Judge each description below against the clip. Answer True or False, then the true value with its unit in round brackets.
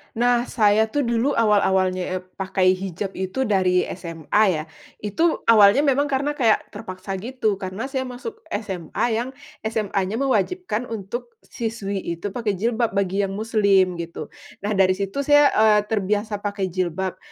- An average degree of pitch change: True (3.9 semitones)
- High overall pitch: True (210 Hz)